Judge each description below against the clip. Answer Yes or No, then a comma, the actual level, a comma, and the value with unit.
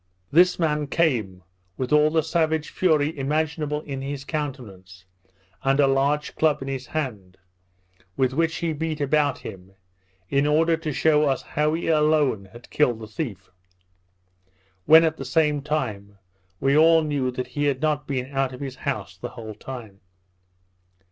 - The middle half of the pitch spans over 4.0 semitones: No, average, 3.3 semitones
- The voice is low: No, medium, 145 Hz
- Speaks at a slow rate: No, average, 160 wpm